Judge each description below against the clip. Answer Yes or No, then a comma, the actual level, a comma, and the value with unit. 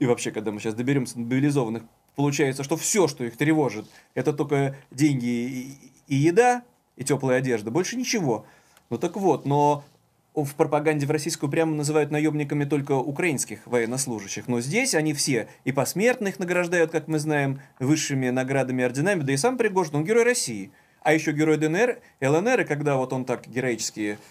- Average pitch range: Yes, average, 3.7 semitones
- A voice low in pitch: No, medium, 145 Hz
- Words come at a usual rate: No, fast, 170 wpm